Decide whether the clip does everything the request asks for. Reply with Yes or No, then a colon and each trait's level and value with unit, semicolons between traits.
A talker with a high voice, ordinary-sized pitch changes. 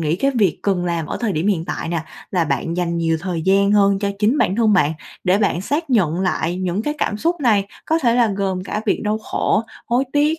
Yes: high, 195 Hz; average, 4.7 semitones